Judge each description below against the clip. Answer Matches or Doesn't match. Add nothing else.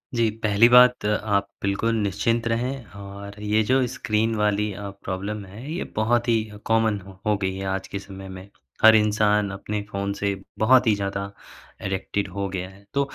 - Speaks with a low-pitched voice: Matches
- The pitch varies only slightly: Matches